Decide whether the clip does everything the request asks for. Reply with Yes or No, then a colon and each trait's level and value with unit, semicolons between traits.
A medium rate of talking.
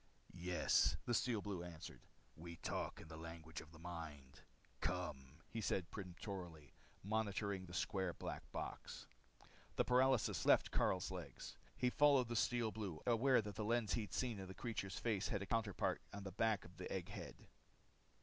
Yes: average, 175 wpm